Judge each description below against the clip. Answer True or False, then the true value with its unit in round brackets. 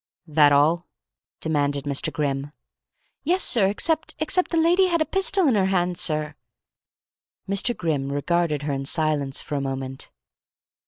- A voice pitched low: False (160 Hz)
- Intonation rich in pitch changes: True (8.9 semitones)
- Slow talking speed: False (155 wpm)